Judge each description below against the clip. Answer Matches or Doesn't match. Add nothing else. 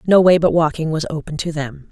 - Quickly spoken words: Matches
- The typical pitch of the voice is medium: Matches